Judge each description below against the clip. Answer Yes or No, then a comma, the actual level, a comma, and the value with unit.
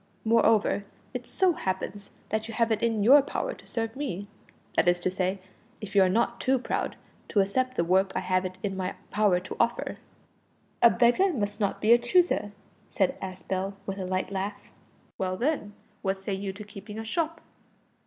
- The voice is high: Yes, high, 205 Hz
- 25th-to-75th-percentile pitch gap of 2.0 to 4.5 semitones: Yes, average, 3.7 semitones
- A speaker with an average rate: Yes, average, 195 wpm